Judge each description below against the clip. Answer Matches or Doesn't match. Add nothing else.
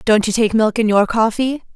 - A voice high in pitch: Matches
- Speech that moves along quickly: Matches